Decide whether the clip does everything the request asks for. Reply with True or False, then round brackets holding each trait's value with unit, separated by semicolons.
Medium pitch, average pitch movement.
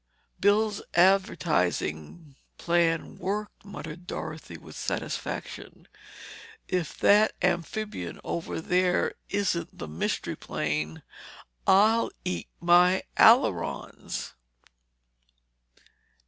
True (180 Hz; 3.6 semitones)